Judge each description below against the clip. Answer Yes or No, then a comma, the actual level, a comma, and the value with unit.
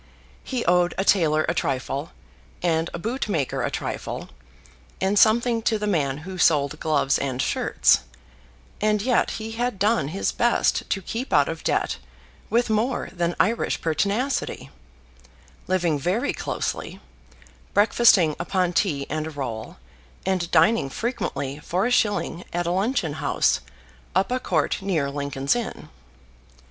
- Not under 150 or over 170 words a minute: No, average, 140 wpm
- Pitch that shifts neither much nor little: No, wide, 6.1 semitones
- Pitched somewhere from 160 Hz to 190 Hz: Yes, medium, 185 Hz